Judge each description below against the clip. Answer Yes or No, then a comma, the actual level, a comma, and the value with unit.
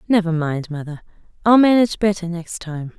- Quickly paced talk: No, average, 160 wpm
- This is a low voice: No, medium, 180 Hz